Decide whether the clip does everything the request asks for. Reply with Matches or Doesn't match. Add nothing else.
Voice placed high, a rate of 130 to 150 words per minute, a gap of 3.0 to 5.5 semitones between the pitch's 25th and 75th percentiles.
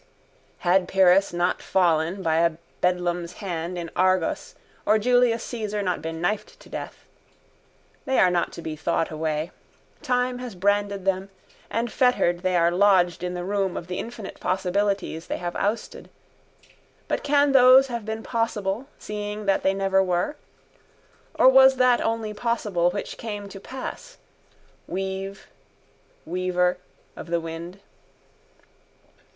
Matches